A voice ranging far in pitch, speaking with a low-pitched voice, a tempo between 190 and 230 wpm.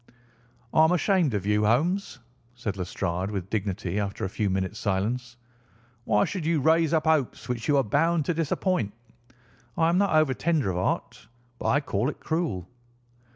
No: wide, 8.2 semitones; low, 125 Hz; average, 175 wpm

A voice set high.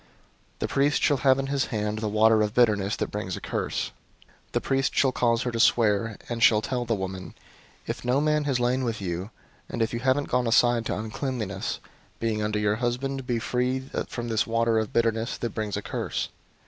No: low, 115 Hz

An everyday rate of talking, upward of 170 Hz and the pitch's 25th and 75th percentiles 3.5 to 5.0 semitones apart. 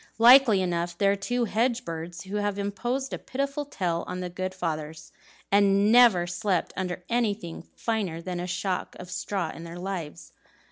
Yes: average, 170 wpm; high, 190 Hz; average, 4.0 semitones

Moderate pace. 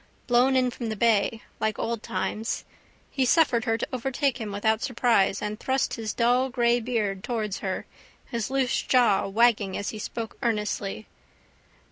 Yes: average, 160 wpm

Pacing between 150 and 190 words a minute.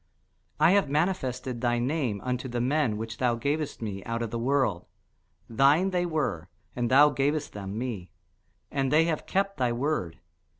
Yes: average, 170 wpm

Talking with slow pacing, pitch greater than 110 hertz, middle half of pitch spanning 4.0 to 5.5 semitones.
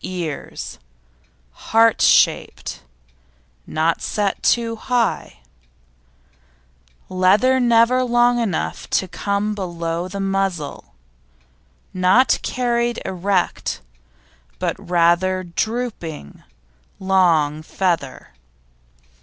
Yes: slow, 75 wpm; high, 190 Hz; average, 5.0 semitones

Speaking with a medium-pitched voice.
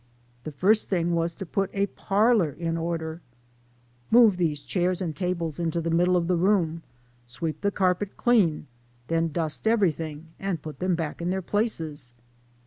Yes: medium, 170 Hz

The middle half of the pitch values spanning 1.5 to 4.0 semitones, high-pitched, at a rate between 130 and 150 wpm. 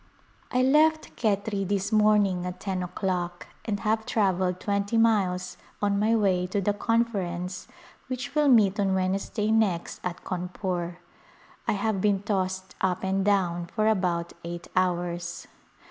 Yes: average, 2.8 semitones; high, 195 Hz; average, 145 wpm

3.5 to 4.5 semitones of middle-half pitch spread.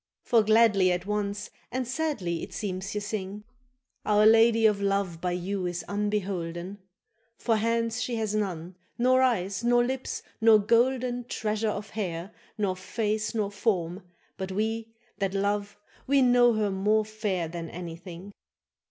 No: average, 3.1 semitones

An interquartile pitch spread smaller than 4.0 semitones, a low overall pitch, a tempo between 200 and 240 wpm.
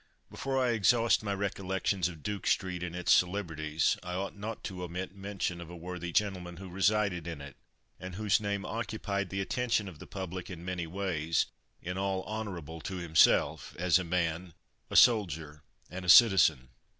No: average, 2.8 semitones; very low, 95 Hz; average, 175 wpm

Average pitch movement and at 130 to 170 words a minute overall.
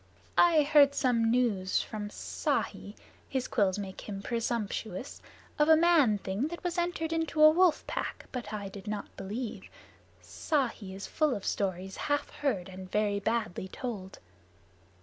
No: wide, 6.8 semitones; average, 150 wpm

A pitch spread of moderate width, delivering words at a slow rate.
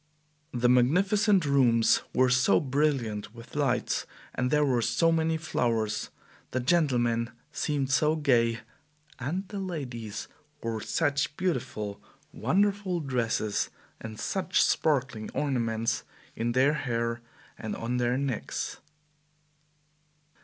Yes: average, 4.6 semitones; slow, 110 wpm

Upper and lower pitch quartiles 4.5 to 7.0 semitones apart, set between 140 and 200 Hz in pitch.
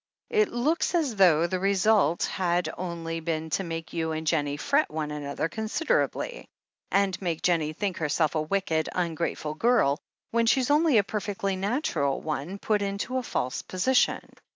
Yes: wide, 5.4 semitones; medium, 185 Hz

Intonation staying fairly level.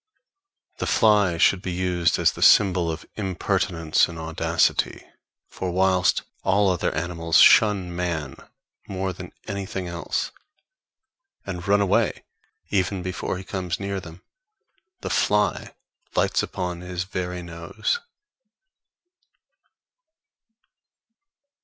Yes: narrow, 1.9 semitones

